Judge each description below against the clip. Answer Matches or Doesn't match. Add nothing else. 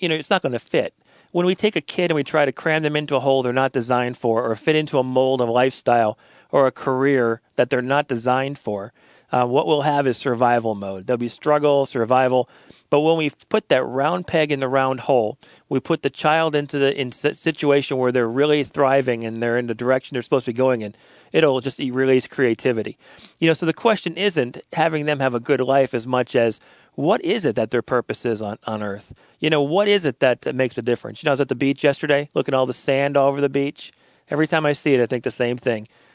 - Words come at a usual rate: Doesn't match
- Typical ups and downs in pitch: Matches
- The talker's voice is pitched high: Doesn't match